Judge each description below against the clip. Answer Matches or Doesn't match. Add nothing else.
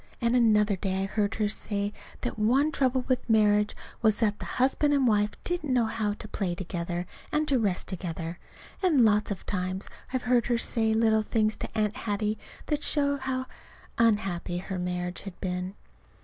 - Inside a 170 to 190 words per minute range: Matches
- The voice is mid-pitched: Doesn't match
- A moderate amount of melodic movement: Matches